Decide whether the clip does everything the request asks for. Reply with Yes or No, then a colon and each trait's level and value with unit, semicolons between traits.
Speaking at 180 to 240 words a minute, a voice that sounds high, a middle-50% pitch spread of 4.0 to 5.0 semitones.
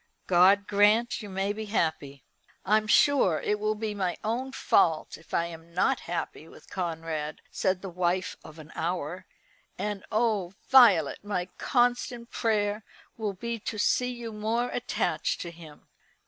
No: average, 155 wpm; high, 200 Hz; average, 4.4 semitones